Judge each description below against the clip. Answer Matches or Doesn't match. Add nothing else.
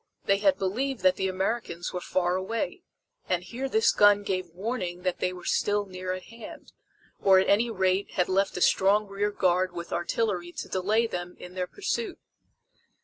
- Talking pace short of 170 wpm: Doesn't match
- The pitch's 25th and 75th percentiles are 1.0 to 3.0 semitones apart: Matches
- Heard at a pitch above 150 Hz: Matches